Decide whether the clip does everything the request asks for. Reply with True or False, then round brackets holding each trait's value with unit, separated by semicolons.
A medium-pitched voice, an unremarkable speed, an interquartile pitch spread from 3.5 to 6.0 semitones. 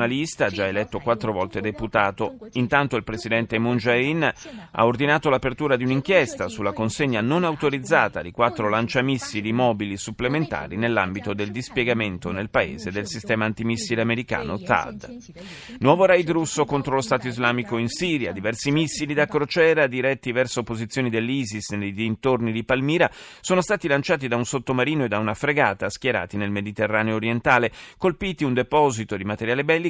False (120 Hz; 155 wpm; 4.6 semitones)